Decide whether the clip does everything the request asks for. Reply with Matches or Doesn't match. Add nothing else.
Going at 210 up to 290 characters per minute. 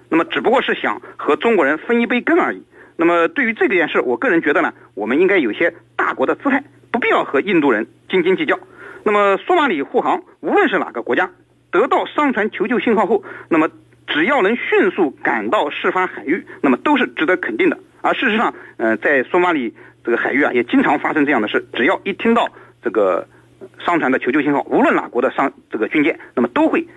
Doesn't match